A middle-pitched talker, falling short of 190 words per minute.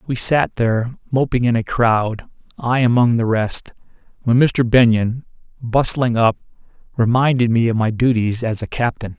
No: low, 120 Hz; average, 155 wpm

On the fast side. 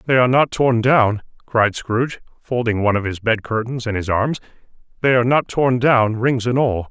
Yes: fast, 210 wpm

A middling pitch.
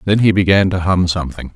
No: very low, 90 Hz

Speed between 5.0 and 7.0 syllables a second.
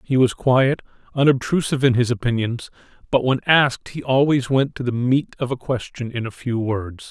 Yes: 5.2 syllables/s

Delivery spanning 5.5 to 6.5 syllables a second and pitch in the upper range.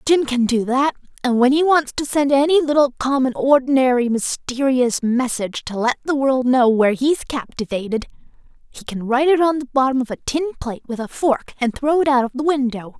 Yes: 5.6 syllables/s; very high, 265 Hz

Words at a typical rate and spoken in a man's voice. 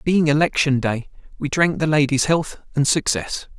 Yes: average, 165 wpm; male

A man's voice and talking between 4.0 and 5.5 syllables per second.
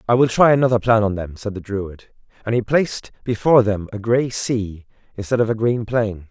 Yes: male; 5.4 syllables/s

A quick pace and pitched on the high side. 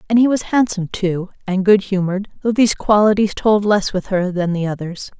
Yes: fast, 210 wpm; high, 200 Hz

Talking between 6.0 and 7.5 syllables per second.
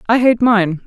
No: 4.5 syllables/s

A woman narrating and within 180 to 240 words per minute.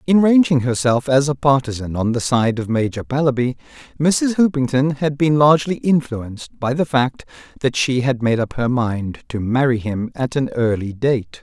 No: male; average, 185 wpm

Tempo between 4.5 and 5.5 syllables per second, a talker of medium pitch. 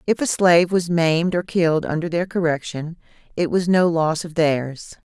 Yes: 4.9 syllables/s; medium, 170 Hz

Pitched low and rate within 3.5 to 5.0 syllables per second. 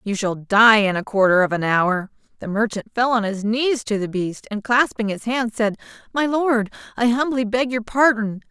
No: high, 220 Hz; 4.7 syllables/s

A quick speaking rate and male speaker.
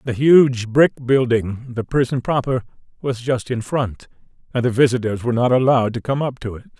No: average, 195 wpm; male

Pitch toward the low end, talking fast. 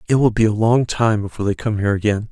Yes: low, 110 Hz; fast, 285 wpm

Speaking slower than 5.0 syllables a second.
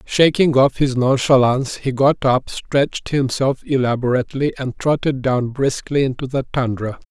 Yes: 4.8 syllables/s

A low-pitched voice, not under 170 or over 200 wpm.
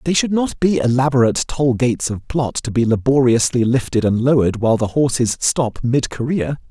Yes: low, 125 Hz; average, 190 wpm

